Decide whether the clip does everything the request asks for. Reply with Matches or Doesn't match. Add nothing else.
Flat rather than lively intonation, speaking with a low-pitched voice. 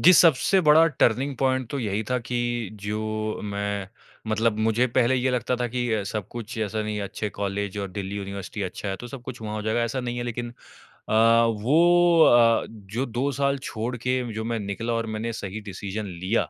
Doesn't match